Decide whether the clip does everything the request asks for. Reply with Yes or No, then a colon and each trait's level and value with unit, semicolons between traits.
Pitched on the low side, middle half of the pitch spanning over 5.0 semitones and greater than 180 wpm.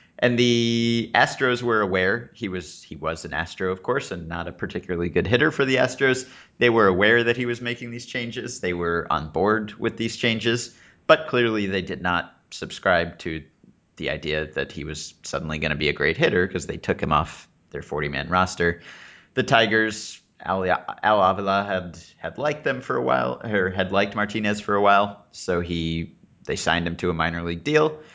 Yes: very low, 95 Hz; wide, 5.5 semitones; average, 200 wpm